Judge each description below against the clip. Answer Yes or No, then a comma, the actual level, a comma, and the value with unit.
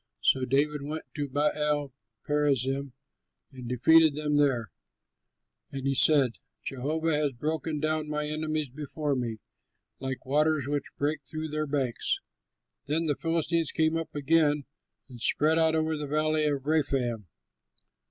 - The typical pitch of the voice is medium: Yes, medium, 150 Hz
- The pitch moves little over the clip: Yes, narrow, 2.3 semitones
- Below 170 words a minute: Yes, average, 140 wpm